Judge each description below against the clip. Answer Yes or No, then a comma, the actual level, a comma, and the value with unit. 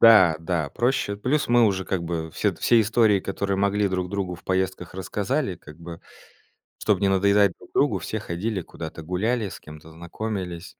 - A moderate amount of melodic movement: Yes, average, 3.3 semitones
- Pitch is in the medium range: No, very low, 95 Hz